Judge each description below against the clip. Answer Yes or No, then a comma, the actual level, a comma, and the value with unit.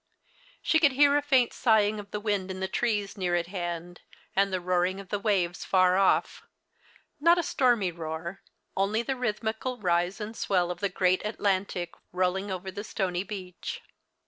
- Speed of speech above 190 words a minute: Yes, average, 200 wpm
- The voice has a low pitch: No, high, 195 Hz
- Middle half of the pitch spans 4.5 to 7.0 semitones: No, average, 3.2 semitones